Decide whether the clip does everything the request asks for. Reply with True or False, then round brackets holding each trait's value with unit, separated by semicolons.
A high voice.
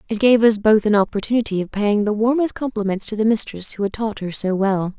True (215 Hz)